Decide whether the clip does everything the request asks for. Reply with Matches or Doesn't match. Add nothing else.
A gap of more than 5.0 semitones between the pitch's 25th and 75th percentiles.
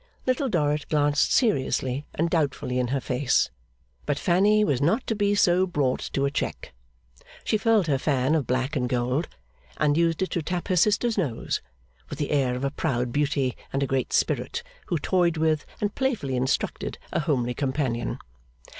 Matches